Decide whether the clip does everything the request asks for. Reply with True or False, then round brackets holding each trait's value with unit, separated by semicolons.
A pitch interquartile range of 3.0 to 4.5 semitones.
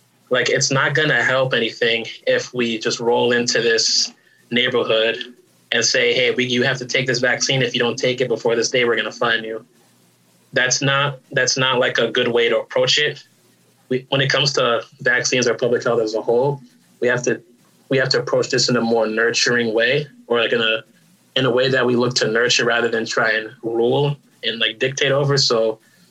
True (3.4 semitones)